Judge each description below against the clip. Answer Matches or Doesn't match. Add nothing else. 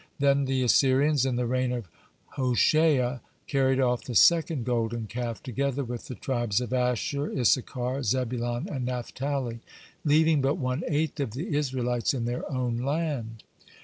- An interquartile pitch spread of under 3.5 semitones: Matches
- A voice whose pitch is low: Matches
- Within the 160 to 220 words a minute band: Doesn't match